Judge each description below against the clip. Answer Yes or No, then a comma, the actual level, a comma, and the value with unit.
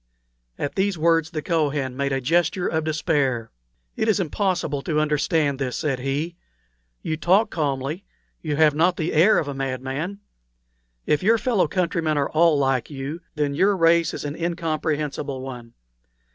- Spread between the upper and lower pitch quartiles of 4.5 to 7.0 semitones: No, average, 3.5 semitones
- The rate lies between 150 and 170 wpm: Yes, average, 160 wpm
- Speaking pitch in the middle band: Yes, medium, 155 Hz